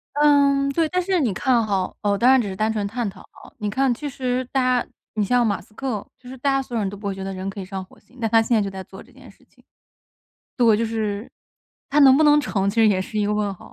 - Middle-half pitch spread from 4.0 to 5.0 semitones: Yes, average, 4.6 semitones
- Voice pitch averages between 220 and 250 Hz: Yes, high, 225 Hz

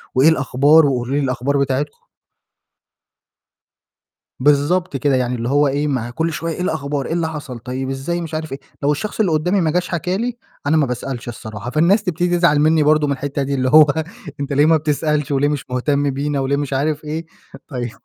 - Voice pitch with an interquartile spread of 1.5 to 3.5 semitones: Yes, average, 2.9 semitones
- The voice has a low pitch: No, medium, 145 Hz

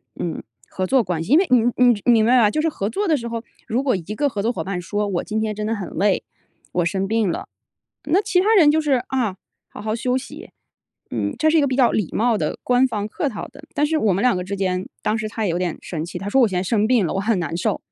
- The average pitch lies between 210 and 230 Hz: Yes, high, 220 Hz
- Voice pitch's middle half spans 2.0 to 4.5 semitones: No, average, 4.9 semitones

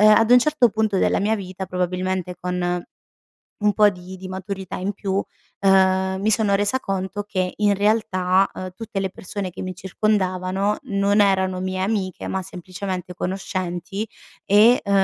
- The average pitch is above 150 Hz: Yes, high, 190 Hz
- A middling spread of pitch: No, narrow, 1.9 semitones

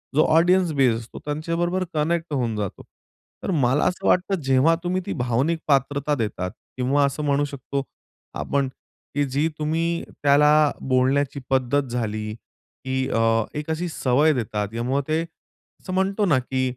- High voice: No, medium, 140 Hz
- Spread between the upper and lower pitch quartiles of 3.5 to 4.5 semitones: Yes, average, 3.9 semitones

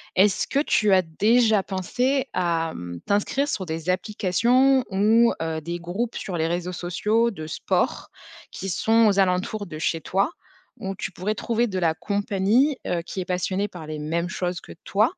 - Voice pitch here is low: No, high, 190 Hz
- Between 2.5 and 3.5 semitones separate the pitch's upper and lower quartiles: No, average, 4.1 semitones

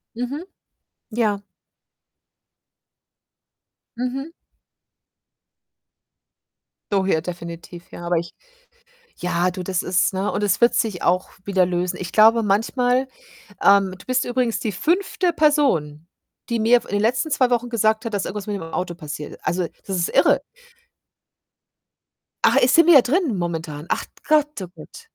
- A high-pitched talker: Yes, high, 205 Hz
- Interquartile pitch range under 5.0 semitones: No, wide, 5.6 semitones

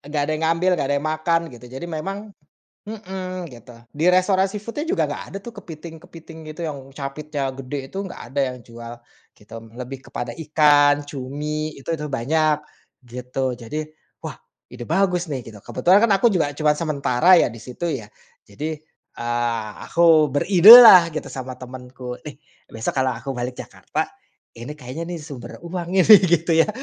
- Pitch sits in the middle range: Yes, medium, 150 Hz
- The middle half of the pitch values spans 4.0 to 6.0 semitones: Yes, average, 4.9 semitones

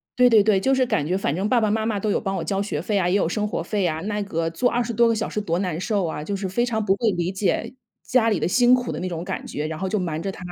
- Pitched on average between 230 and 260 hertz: No, high, 200 Hz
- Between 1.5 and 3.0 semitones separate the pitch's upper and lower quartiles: No, average, 3.8 semitones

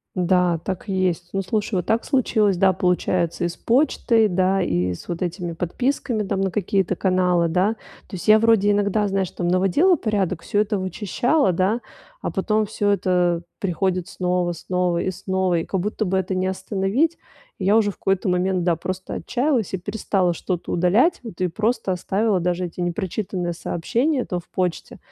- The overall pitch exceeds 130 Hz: Yes, high, 190 Hz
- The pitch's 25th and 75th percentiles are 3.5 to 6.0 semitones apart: No, average, 2.8 semitones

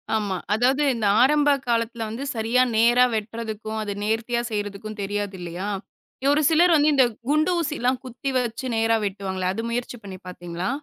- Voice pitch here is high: Yes, high, 225 Hz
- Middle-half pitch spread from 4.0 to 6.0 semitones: No, average, 3.4 semitones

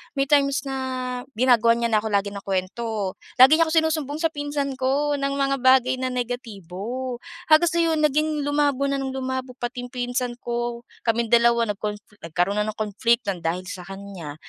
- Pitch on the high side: Yes, very high, 250 Hz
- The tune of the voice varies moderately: Yes, average, 4.3 semitones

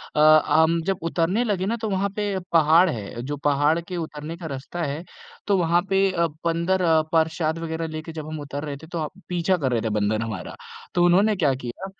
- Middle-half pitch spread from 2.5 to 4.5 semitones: Yes, average, 3.5 semitones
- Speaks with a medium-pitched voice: Yes, medium, 165 Hz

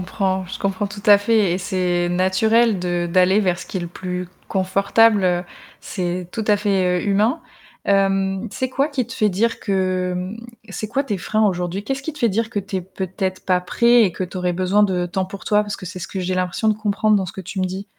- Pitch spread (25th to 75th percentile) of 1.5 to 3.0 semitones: Yes, narrow, 2.4 semitones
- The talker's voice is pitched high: Yes, high, 195 Hz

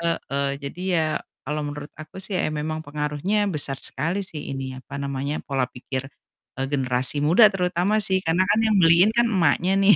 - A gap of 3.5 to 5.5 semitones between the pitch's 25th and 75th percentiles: Yes, average, 4.2 semitones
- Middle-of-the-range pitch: Yes, medium, 155 Hz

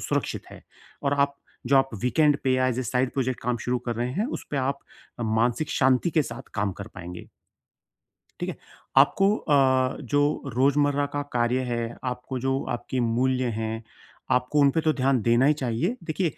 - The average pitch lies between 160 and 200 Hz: No, low, 130 Hz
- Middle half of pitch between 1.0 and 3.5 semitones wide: Yes, average, 2.8 semitones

